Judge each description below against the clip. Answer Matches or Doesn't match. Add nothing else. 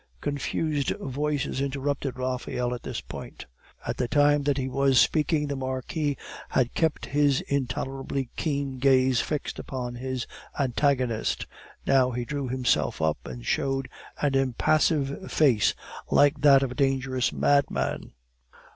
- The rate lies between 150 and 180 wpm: Doesn't match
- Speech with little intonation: Matches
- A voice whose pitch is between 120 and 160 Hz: Matches